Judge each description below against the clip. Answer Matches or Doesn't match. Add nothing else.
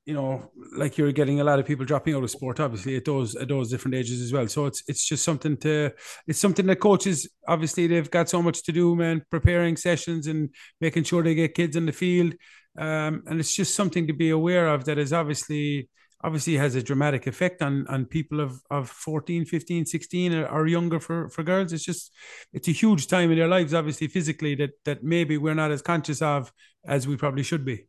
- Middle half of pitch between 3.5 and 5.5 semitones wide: Doesn't match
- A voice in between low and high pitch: Matches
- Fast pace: Matches